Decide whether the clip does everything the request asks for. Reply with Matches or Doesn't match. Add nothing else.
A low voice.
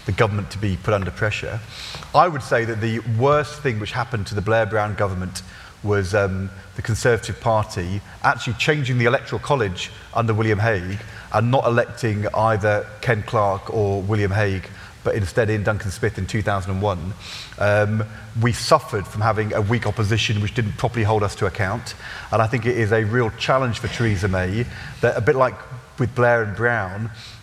Matches